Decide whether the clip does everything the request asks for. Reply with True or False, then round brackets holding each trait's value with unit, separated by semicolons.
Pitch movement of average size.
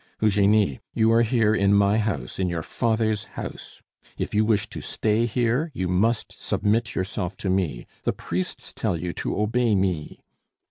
True (3.2 semitones)